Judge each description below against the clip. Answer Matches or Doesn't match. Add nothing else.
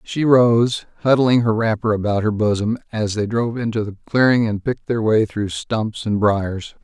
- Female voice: Doesn't match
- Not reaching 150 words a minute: Doesn't match